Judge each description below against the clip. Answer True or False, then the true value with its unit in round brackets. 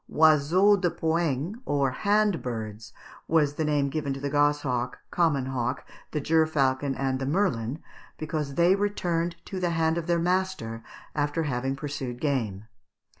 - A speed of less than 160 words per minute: True (150 wpm)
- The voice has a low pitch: False (145 Hz)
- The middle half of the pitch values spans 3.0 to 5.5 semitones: True (4.1 semitones)